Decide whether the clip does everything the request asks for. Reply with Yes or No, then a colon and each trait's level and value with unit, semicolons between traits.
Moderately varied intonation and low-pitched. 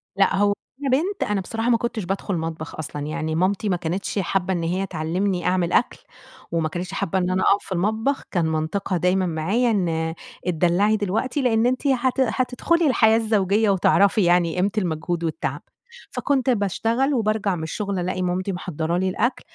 No: average, 4.3 semitones; high, 195 Hz